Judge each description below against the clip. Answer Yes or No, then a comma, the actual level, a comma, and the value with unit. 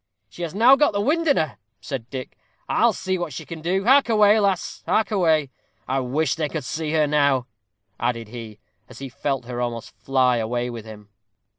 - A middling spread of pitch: No, wide, 7.3 semitones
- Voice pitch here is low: No, medium, 150 Hz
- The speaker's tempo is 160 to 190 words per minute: No, average, 200 wpm